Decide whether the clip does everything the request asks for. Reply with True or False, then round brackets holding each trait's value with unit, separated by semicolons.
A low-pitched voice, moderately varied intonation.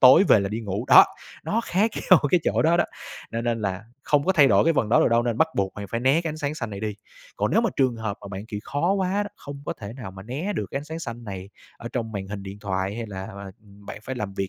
False (115 Hz; 6.2 semitones)